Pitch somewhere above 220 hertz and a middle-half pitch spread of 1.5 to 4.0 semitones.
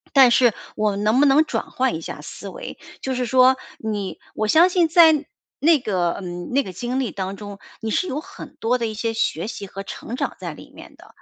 No: high, 240 Hz; average, 4.8 semitones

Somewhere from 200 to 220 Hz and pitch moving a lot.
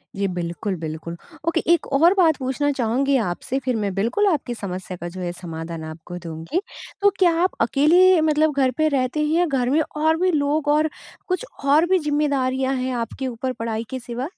No: very high, 265 Hz; wide, 7.2 semitones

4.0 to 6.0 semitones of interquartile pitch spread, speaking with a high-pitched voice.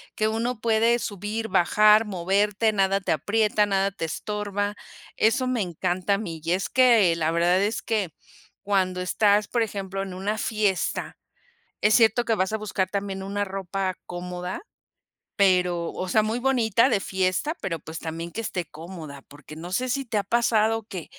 No: average, 3.2 semitones; high, 200 Hz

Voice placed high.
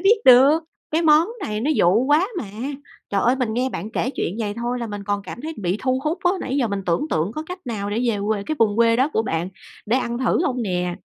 Yes: high, 235 Hz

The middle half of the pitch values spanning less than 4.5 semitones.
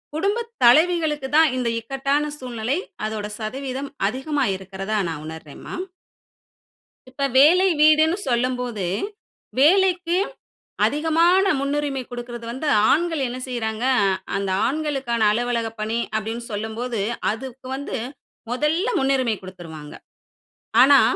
No: average, 5.0 semitones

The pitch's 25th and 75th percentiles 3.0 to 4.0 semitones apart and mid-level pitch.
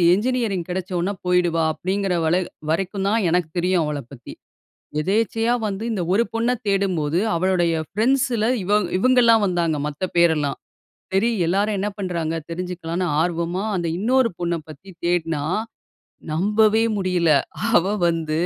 Yes: average, 3.6 semitones; medium, 180 Hz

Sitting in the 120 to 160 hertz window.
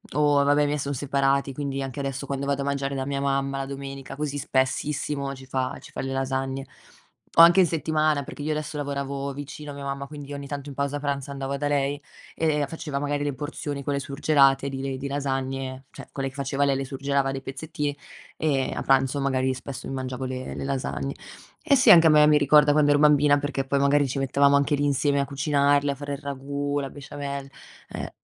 Yes: medium, 140 Hz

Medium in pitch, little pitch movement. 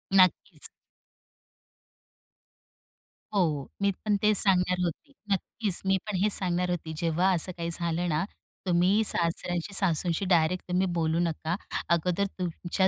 Yes: medium, 180 Hz; narrow, 2.2 semitones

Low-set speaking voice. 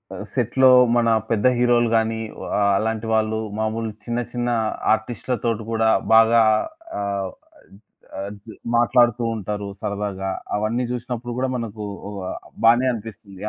Yes: low, 115 Hz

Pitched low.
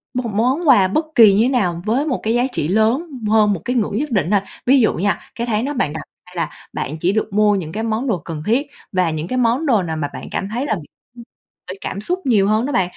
No: high, 215 Hz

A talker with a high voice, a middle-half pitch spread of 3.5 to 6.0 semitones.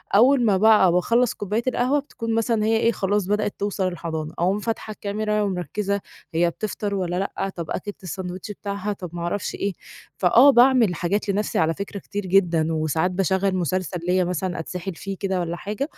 No: high, 195 Hz; average, 2.9 semitones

